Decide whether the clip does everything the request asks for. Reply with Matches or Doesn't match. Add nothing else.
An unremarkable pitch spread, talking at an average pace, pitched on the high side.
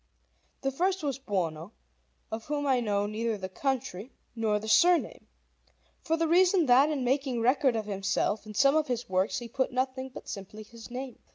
Matches